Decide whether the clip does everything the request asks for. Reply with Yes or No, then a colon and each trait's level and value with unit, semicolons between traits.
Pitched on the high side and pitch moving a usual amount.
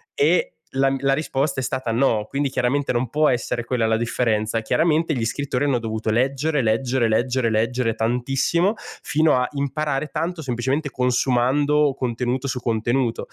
No: low, 130 Hz; average, 3.2 semitones